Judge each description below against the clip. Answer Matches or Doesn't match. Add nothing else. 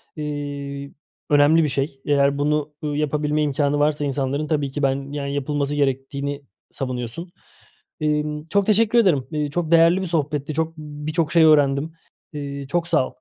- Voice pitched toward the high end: Doesn't match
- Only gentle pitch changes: Matches